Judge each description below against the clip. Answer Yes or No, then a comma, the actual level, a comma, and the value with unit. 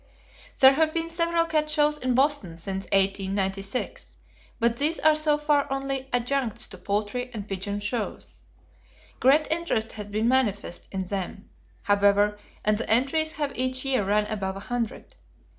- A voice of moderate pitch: No, high, 240 Hz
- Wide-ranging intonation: Yes, wide, 6.3 semitones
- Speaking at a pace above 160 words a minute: No, average, 155 wpm